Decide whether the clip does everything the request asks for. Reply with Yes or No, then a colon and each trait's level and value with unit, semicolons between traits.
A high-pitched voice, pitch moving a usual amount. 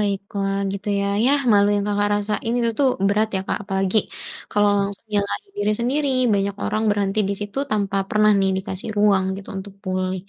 No: high, 205 Hz; narrow, 1.4 semitones